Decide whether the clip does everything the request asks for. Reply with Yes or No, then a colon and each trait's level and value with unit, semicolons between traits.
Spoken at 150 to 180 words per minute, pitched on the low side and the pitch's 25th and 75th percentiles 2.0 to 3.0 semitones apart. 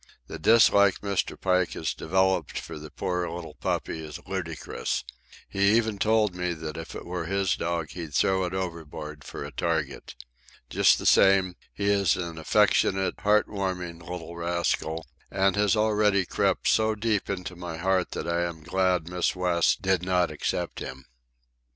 Yes: average, 165 wpm; very low, 90 Hz; average, 2.7 semitones